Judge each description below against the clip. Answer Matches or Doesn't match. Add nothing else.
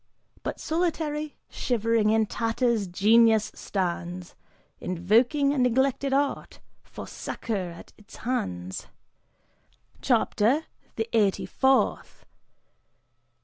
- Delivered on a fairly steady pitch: Doesn't match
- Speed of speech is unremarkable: Doesn't match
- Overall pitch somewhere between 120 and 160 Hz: Doesn't match